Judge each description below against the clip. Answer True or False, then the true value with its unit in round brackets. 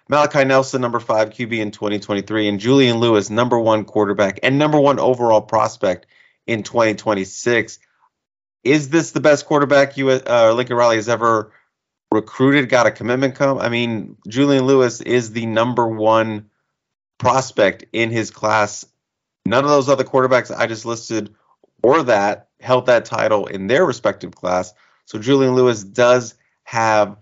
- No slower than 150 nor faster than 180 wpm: True (155 wpm)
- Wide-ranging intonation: False (3.6 semitones)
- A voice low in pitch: True (120 Hz)